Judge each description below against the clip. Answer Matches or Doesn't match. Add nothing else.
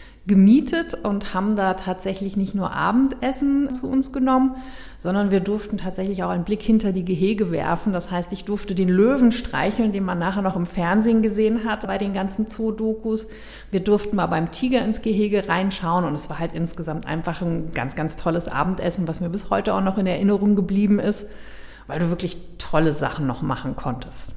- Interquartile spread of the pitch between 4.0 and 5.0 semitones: Doesn't match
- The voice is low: Doesn't match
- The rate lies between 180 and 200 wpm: Matches